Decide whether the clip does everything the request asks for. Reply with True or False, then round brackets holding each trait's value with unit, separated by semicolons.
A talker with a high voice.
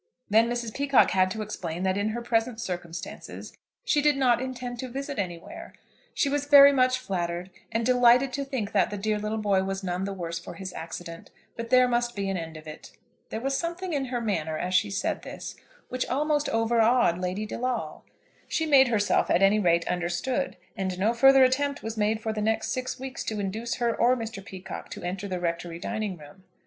True (220 Hz)